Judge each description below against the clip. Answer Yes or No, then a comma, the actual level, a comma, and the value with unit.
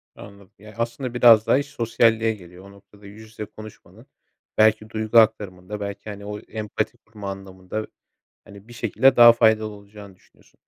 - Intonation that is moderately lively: No, narrow, 1.8 semitones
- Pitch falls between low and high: No, low, 110 Hz